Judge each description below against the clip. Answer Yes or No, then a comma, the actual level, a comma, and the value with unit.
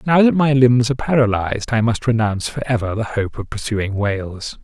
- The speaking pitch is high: No, low, 115 Hz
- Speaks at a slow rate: No, fast, 205 wpm